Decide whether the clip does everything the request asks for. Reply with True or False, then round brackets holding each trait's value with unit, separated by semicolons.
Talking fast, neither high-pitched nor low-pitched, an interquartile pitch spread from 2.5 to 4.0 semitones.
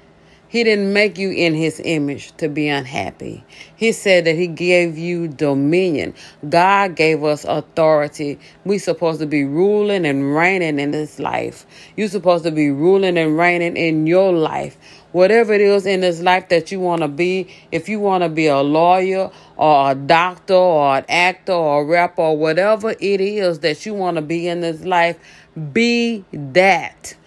False (185 wpm; 170 Hz; 3.4 semitones)